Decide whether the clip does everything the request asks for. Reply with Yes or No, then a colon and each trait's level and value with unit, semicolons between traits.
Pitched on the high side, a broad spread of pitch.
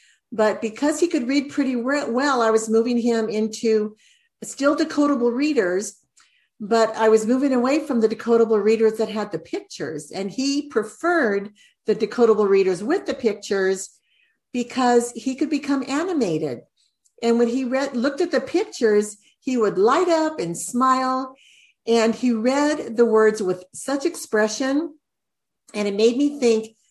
No: high, 240 Hz; average, 4.4 semitones